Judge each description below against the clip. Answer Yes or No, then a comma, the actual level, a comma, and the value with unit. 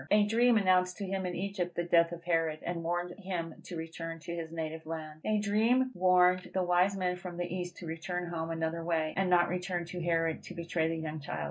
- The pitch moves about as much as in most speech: No, narrow, 1.8 semitones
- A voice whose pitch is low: No, medium, 175 Hz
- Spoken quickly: Yes, fast, 230 wpm